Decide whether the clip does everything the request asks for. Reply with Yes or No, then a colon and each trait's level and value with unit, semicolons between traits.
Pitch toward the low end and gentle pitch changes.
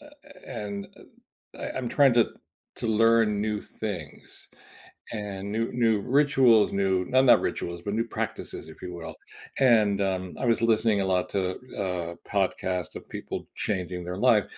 No: low, 105 Hz; average, 3.7 semitones